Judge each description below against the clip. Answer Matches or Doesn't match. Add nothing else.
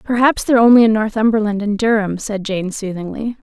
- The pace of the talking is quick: Doesn't match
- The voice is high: Matches